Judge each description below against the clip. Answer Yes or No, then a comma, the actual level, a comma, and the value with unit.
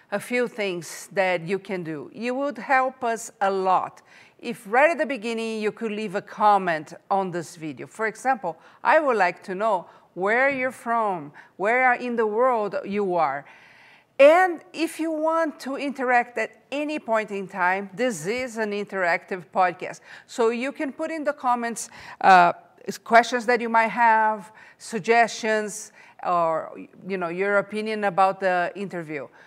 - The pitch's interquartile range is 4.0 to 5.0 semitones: Yes, average, 4.5 semitones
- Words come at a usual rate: Yes, average, 165 wpm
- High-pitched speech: Yes, high, 220 Hz